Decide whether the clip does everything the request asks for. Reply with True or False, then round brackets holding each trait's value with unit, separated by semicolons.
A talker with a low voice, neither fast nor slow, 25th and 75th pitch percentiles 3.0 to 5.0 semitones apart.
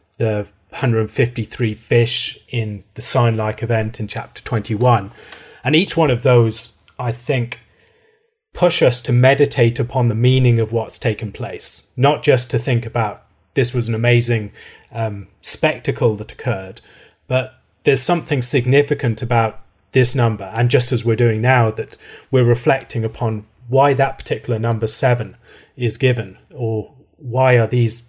False (120 Hz; 145 wpm; 2.5 semitones)